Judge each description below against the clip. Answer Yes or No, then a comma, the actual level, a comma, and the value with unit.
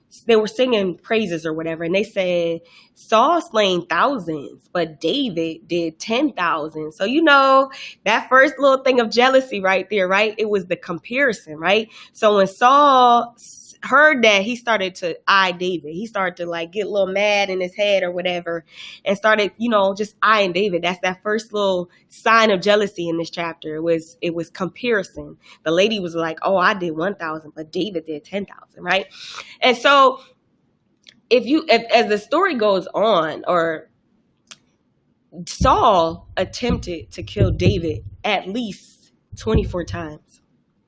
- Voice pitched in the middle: No, high, 195 Hz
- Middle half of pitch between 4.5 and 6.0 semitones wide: Yes, average, 5.2 semitones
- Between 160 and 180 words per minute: Yes, average, 165 wpm